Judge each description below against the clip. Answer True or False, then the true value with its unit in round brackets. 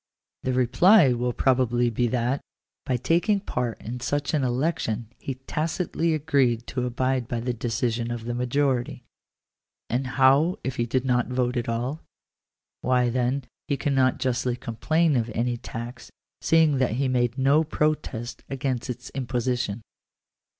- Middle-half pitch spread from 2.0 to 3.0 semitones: True (2.4 semitones)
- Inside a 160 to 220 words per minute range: False (150 wpm)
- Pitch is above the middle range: False (125 Hz)